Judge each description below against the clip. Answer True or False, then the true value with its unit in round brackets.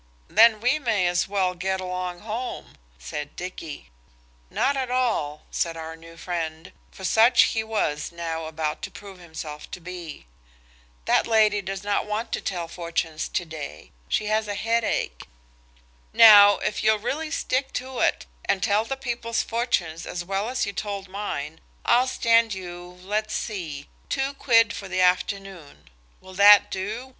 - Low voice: False (195 Hz)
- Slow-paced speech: False (155 wpm)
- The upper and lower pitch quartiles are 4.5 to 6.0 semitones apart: True (4.8 semitones)